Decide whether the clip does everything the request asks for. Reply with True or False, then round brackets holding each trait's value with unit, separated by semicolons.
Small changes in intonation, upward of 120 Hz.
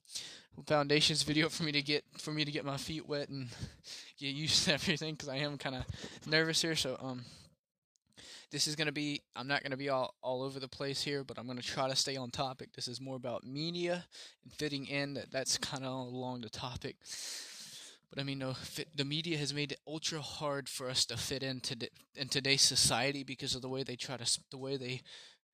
True (2.2 semitones; 140 Hz)